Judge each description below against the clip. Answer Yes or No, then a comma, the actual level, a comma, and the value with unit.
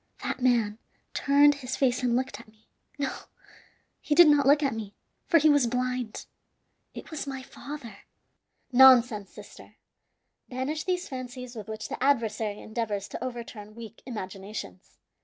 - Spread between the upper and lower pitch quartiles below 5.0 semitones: Yes, average, 4.2 semitones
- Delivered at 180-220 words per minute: No, average, 150 wpm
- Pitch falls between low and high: No, very high, 250 Hz